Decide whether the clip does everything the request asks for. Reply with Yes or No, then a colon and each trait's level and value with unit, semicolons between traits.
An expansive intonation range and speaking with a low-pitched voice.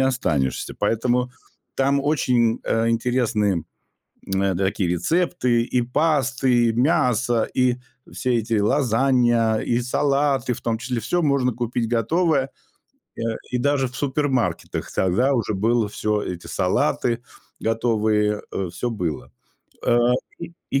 No: average, 3.2 semitones; low, 120 Hz